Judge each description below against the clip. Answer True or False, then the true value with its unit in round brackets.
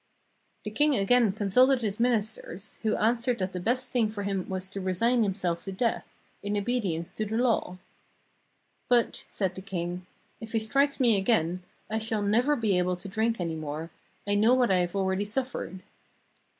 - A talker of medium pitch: False (205 Hz)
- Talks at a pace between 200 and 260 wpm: False (185 wpm)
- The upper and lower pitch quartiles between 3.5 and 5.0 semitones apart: True (3.9 semitones)